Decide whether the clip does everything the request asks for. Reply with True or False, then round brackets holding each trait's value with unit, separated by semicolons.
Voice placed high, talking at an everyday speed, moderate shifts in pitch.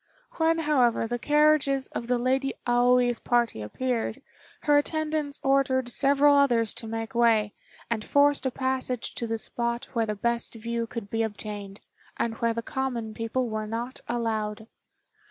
True (240 Hz; 155 wpm; 3.0 semitones)